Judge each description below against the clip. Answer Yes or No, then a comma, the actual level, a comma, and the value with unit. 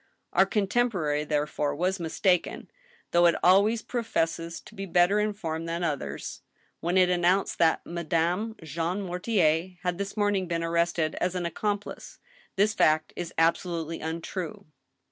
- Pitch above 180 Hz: No, medium, 175 Hz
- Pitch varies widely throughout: No, average, 3.0 semitones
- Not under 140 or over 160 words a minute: Yes, average, 145 wpm